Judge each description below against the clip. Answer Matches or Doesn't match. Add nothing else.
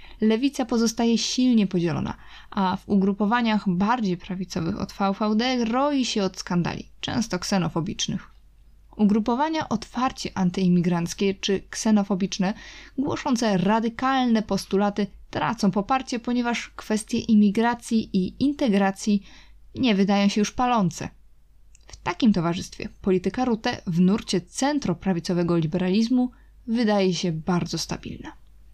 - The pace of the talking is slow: Matches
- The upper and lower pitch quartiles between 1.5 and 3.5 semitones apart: Doesn't match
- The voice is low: Doesn't match